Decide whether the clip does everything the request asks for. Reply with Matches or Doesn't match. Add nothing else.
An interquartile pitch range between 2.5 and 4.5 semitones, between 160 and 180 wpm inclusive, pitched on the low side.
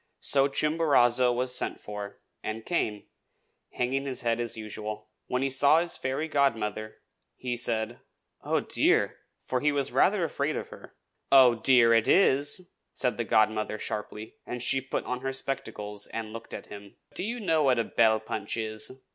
Matches